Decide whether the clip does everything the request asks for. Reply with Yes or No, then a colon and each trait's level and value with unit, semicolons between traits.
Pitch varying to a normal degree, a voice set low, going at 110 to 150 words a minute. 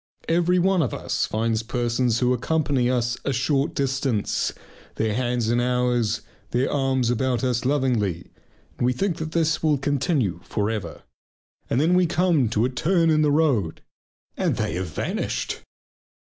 No: average, 4.5 semitones; low, 125 Hz; average, 160 wpm